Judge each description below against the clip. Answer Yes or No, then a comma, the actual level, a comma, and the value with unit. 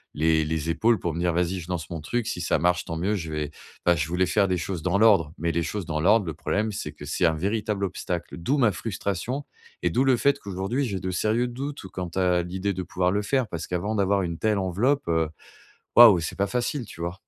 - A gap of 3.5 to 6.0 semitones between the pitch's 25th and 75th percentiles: Yes, average, 4.1 semitones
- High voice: No, very low, 95 Hz